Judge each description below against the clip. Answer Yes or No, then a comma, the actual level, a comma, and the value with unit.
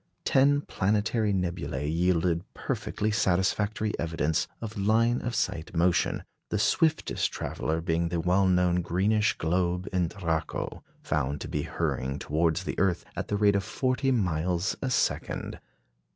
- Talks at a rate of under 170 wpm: Yes, average, 140 wpm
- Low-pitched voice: Yes, very low, 90 Hz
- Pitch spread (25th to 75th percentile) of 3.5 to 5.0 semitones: Yes, average, 4.1 semitones